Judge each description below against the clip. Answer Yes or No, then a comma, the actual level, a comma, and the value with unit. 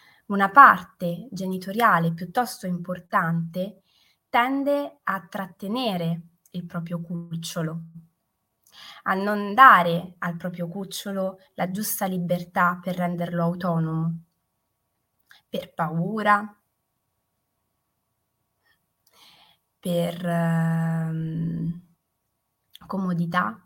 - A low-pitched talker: No, medium, 180 Hz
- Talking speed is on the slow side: Yes, slow, 70 wpm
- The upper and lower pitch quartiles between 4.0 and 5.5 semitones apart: No, narrow, 2.6 semitones